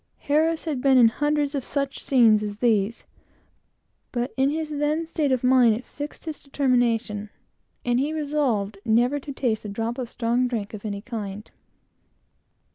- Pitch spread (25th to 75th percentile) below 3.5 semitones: No, average, 4.4 semitones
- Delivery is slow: No, average, 175 wpm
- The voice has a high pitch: Yes, very high, 250 Hz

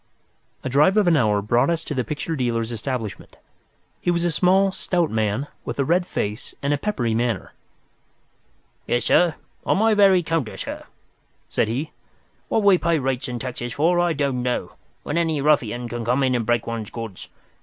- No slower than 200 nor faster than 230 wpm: No, average, 185 wpm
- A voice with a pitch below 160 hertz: Yes, low, 135 Hz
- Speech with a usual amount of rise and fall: No, wide, 6.2 semitones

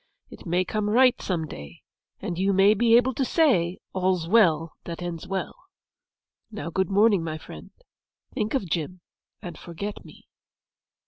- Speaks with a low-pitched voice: No, high, 190 Hz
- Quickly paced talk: No, average, 155 wpm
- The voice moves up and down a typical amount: Yes, average, 4.2 semitones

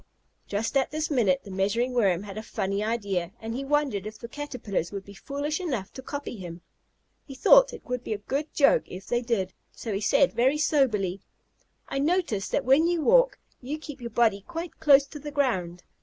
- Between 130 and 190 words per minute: No, fast, 205 wpm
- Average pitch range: No, wide, 6.4 semitones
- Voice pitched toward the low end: No, high, 245 Hz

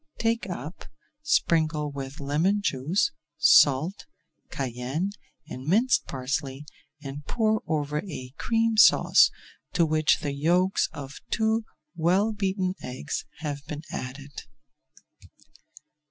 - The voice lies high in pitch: No, medium, 155 Hz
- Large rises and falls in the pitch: Yes, wide, 5.9 semitones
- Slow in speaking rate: Yes, slow, 115 wpm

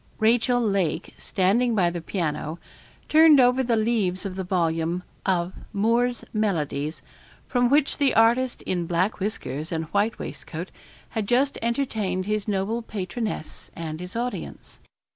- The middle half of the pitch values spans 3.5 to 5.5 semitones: Yes, average, 5.1 semitones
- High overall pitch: Yes, high, 205 Hz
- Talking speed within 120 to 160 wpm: Yes, average, 140 wpm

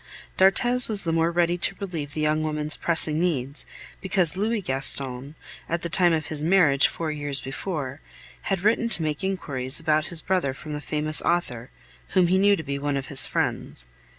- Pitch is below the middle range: No, medium, 160 Hz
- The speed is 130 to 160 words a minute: No, average, 190 wpm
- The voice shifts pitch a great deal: No, average, 3.8 semitones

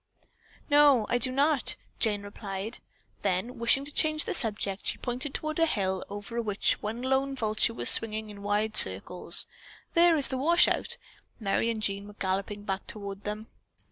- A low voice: No, high, 220 Hz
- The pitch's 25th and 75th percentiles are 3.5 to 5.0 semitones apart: Yes, average, 4.6 semitones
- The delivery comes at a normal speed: Yes, average, 170 wpm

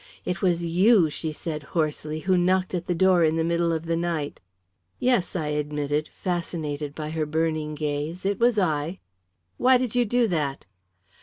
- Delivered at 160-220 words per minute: Yes, average, 175 wpm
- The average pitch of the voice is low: No, medium, 165 Hz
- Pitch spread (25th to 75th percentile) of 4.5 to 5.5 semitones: No, average, 3.2 semitones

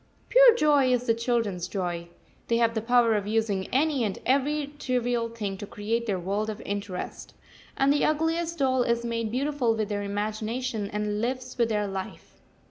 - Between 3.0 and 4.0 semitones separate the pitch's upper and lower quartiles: Yes, average, 3.7 semitones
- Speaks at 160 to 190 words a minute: Yes, average, 180 wpm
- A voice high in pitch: Yes, high, 230 Hz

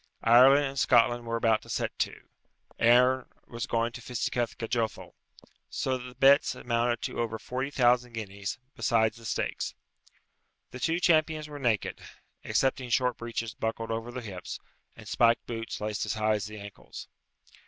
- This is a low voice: Yes, low, 120 Hz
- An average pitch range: No, narrow, 2.1 semitones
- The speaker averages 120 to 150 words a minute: No, average, 165 wpm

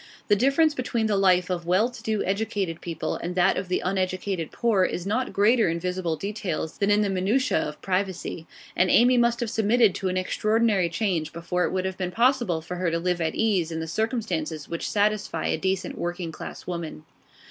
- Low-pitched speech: No, high, 190 Hz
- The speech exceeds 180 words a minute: Yes, fast, 205 wpm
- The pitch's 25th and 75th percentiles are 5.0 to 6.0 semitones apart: No, average, 3.8 semitones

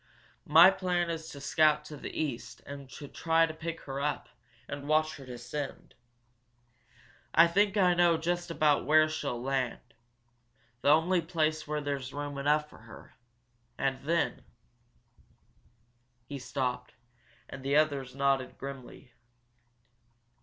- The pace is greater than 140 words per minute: No, slow, 135 wpm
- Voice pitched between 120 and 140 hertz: No, medium, 150 Hz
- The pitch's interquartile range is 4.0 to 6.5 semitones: No, average, 3.1 semitones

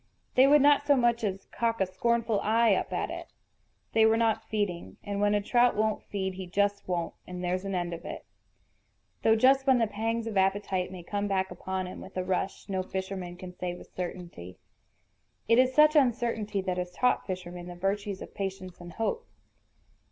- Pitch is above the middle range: Yes, high, 200 Hz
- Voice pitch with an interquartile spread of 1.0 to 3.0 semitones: No, average, 3.8 semitones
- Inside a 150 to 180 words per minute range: No, average, 200 wpm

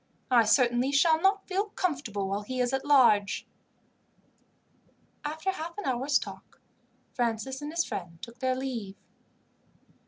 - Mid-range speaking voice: No, very high, 260 Hz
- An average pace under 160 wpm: Yes, slow, 135 wpm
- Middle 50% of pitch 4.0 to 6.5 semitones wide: Yes, average, 5.2 semitones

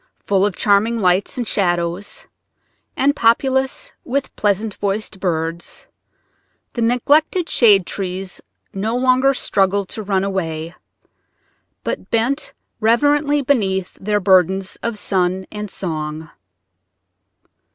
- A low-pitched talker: No, high, 205 Hz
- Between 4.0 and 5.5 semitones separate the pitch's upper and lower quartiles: Yes, average, 4.5 semitones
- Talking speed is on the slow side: Yes, slow, 110 wpm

